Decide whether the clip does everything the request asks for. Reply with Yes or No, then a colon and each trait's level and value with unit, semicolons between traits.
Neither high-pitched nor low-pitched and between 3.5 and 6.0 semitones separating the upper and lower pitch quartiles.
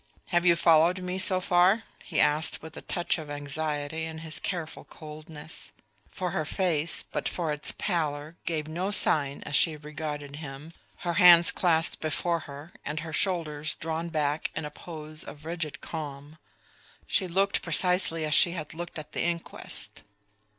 No: medium, 160 Hz; narrow, 2.4 semitones